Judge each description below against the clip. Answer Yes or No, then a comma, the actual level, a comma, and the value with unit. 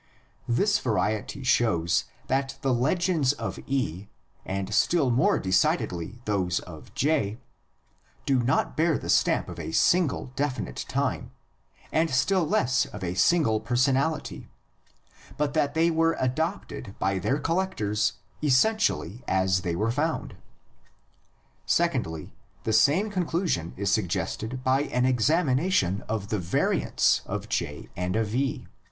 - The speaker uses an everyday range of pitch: No, wide, 7.3 semitones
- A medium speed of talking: No, slow, 130 wpm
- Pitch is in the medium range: No, low, 125 Hz